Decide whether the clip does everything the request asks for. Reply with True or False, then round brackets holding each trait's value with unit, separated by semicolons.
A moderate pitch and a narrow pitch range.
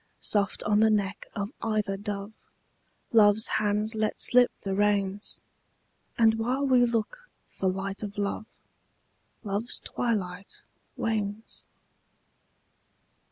False (210 Hz; 1.8 semitones)